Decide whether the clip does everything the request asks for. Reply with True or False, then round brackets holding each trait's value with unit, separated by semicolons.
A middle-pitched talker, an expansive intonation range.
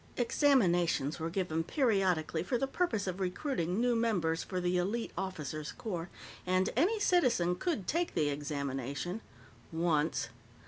True (180 Hz; 6.2 semitones)